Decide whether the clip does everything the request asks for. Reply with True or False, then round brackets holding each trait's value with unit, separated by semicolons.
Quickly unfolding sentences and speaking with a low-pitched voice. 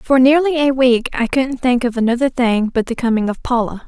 False (230 wpm; 250 Hz)